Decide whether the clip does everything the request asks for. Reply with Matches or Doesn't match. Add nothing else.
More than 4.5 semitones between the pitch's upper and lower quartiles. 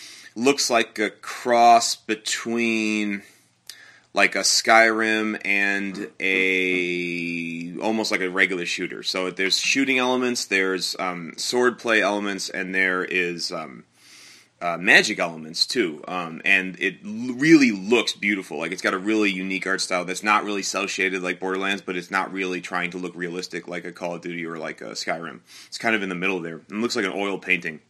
Doesn't match